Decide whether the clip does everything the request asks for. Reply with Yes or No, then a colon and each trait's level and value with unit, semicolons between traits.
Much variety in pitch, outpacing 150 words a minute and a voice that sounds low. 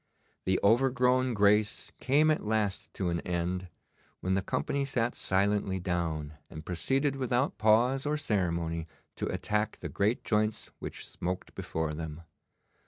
No: wide, 6.0 semitones; average, 140 wpm; low, 105 Hz